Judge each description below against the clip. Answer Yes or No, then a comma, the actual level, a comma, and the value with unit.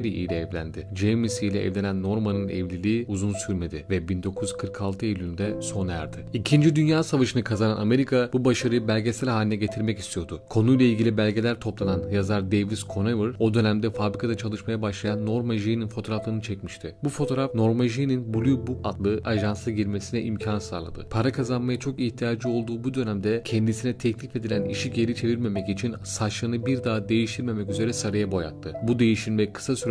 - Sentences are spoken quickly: Yes, fast, 155 wpm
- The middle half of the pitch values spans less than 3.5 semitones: Yes, average, 2.9 semitones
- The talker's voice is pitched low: Yes, low, 110 Hz